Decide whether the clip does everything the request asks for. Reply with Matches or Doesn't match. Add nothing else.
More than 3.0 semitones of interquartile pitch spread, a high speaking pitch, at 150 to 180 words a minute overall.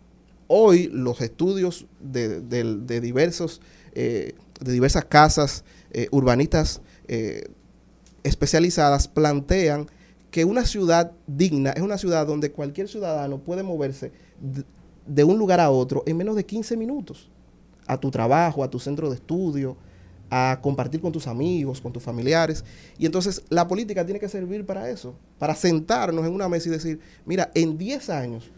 Doesn't match